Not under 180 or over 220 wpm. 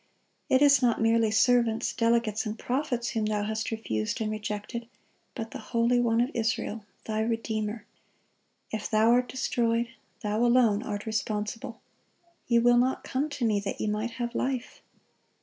No: average, 160 wpm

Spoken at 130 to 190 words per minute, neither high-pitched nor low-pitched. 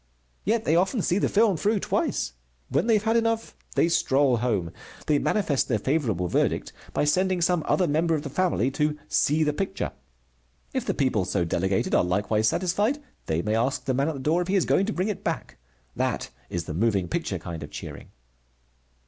No: fast, 205 wpm; medium, 150 Hz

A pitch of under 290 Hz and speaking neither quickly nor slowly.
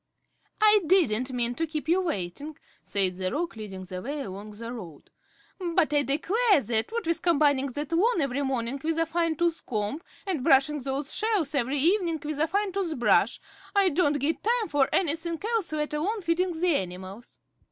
No: very high, 300 Hz; average, 185 wpm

